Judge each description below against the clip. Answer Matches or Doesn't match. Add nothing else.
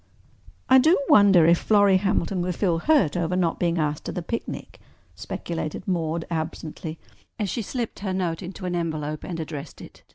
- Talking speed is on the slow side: Doesn't match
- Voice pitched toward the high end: Doesn't match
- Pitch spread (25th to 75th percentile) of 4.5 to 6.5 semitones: Doesn't match